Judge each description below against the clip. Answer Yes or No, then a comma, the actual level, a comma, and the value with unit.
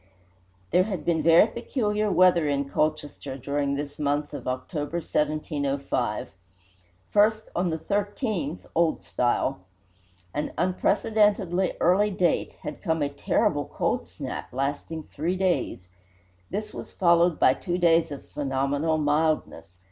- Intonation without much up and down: No, average, 4.4 semitones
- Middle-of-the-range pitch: Yes, medium, 160 Hz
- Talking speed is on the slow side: Yes, slow, 125 wpm